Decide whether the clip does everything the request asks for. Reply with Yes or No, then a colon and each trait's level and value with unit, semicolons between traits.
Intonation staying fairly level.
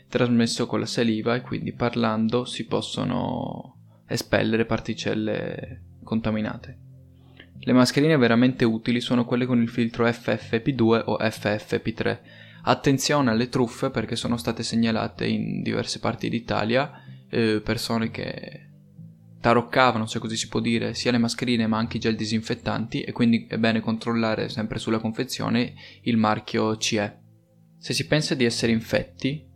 Yes: narrow, 2.1 semitones